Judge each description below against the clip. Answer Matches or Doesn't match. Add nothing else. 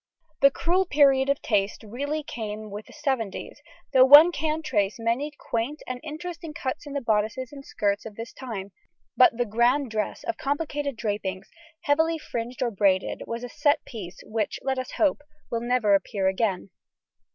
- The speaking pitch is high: Matches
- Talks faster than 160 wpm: Matches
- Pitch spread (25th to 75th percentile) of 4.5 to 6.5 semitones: Matches